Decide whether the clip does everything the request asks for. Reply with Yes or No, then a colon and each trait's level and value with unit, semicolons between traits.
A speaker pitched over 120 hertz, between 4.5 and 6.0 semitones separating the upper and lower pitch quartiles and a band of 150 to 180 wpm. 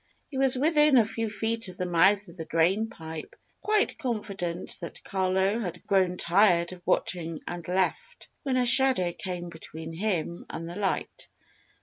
Yes: high, 190 Hz; average, 4.9 semitones; average, 165 wpm